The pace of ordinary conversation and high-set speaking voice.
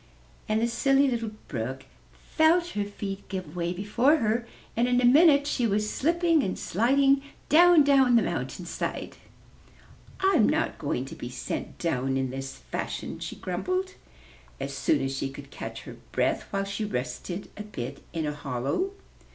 Yes: average, 165 wpm; high, 210 Hz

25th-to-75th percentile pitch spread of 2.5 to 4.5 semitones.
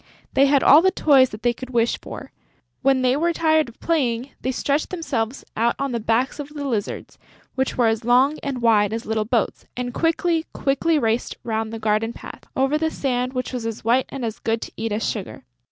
Yes: average, 3.7 semitones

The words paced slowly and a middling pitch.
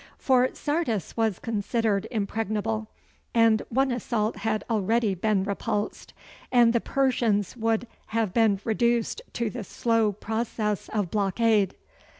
No: slow, 125 wpm; high, 220 Hz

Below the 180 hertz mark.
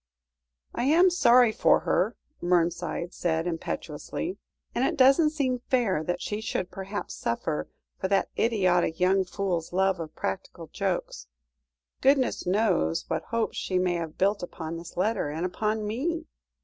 No: high, 190 Hz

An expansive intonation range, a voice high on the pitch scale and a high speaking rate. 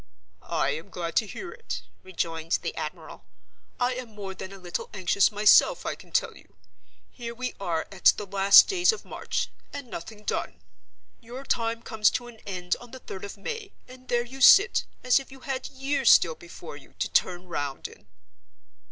No: wide, 6.1 semitones; high, 215 Hz; average, 185 wpm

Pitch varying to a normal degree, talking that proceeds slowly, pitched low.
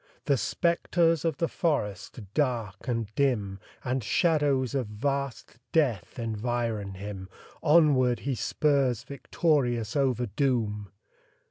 Yes: average, 4.8 semitones; slow, 110 wpm; low, 125 Hz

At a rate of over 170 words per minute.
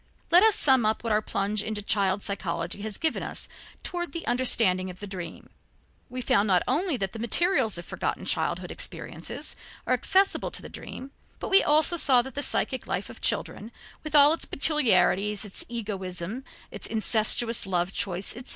Yes: average, 180 wpm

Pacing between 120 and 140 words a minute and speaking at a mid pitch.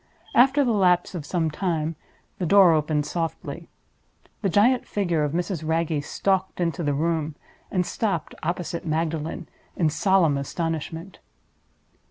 Yes: slow, 135 wpm; medium, 170 Hz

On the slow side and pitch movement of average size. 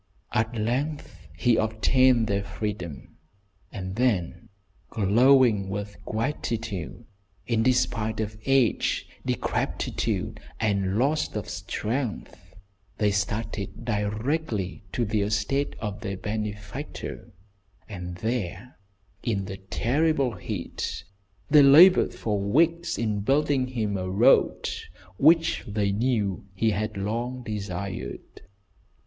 Yes: slow, 105 wpm; average, 3.9 semitones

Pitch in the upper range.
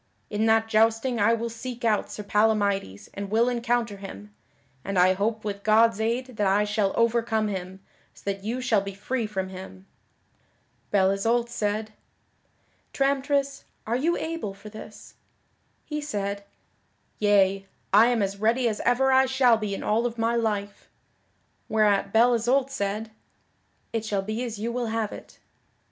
Yes: high, 220 Hz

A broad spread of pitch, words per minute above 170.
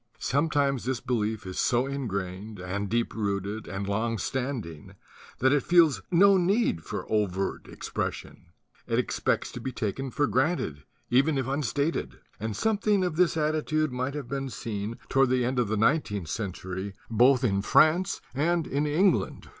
No: wide, 6.4 semitones; average, 150 wpm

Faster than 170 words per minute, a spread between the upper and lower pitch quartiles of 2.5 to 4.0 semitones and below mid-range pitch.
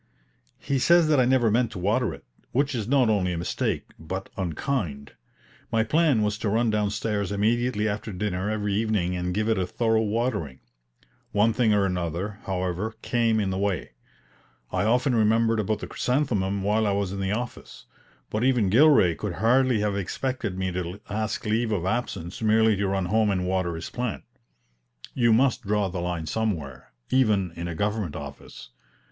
Yes: average, 180 wpm; average, 3.4 semitones; low, 105 Hz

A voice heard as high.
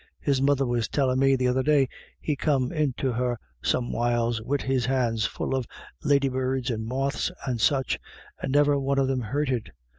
No: low, 130 Hz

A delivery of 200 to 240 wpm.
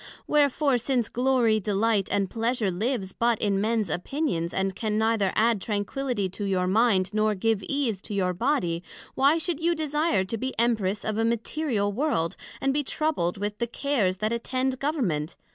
No: average, 180 wpm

